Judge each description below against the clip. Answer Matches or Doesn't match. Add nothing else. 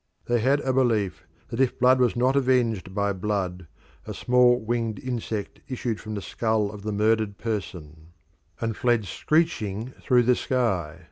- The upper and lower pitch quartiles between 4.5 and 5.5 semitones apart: Doesn't match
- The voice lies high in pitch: Doesn't match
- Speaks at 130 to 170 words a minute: Matches